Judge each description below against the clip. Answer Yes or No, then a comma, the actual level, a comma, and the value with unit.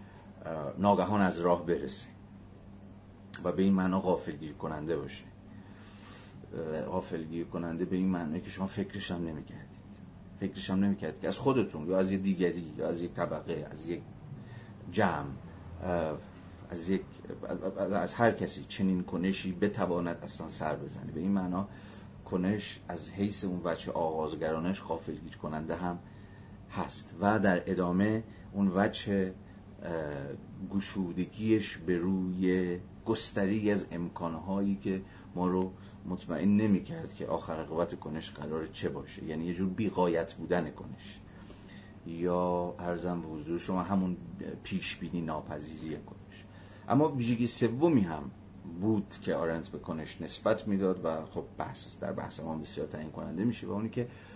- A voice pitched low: Yes, very low, 95 Hz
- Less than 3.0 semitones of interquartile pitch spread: Yes, narrow, 2.5 semitones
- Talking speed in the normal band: No, fast, 140 wpm